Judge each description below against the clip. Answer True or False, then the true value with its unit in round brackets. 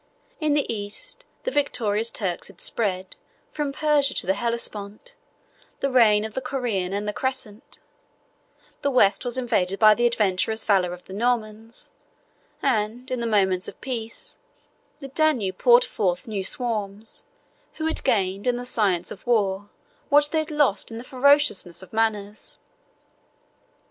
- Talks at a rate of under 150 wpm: False (155 wpm)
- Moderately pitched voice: False (225 Hz)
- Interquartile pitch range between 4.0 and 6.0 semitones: True (4.4 semitones)